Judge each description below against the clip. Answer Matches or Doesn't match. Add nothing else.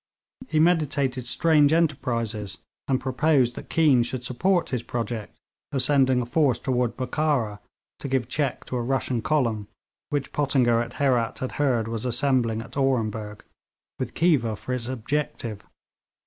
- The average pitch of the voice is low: Matches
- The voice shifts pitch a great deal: Doesn't match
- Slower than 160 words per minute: Matches